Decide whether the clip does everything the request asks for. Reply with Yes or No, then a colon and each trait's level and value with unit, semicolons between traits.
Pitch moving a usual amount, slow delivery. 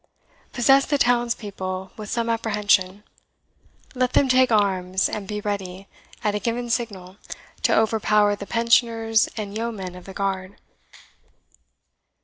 Yes: average, 3.2 semitones; slow, 130 wpm